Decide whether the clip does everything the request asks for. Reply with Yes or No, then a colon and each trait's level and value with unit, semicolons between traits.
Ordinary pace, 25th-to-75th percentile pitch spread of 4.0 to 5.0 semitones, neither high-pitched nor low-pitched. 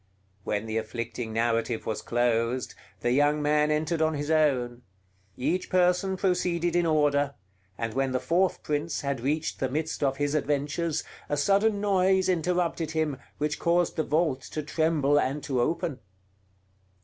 Yes: average, 155 wpm; average, 4.3 semitones; medium, 150 Hz